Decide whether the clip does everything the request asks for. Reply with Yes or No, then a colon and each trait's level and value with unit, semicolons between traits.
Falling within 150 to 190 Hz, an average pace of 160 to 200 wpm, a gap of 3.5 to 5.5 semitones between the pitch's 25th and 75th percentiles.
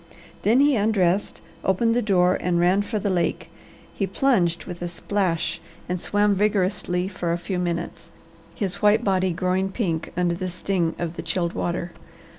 No: medium, 185 Hz; average, 170 wpm; average, 2.7 semitones